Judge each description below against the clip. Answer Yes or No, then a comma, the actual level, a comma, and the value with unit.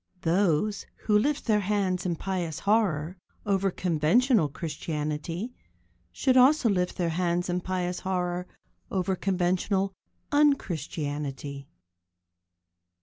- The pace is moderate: No, slow, 105 wpm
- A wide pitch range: No, average, 3.6 semitones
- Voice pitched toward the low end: No, medium, 180 Hz